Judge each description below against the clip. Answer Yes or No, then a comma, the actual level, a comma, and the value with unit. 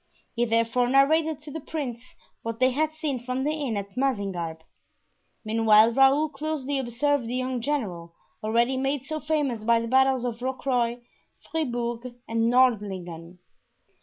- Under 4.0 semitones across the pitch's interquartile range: Yes, average, 3.2 semitones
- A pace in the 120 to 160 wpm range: Yes, average, 145 wpm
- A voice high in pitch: Yes, very high, 250 Hz